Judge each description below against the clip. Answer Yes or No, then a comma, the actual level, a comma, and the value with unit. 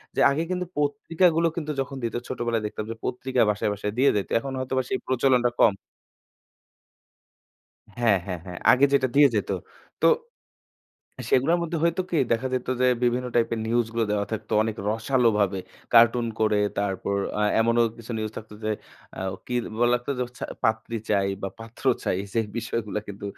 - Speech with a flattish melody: No, average, 3.5 semitones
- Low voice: Yes, low, 115 Hz